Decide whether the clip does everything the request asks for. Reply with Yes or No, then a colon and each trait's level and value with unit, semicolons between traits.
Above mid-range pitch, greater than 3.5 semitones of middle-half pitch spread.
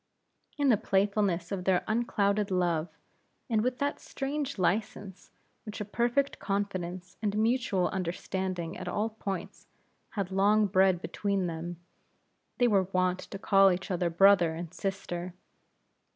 No: high, 195 Hz; average, 2.8 semitones